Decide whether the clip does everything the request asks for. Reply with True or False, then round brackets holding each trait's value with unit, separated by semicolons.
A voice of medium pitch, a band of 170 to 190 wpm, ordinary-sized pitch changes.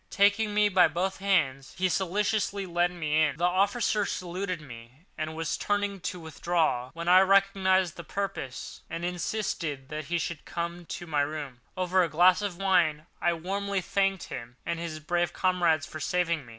True (175 Hz; 175 wpm; 3.5 semitones)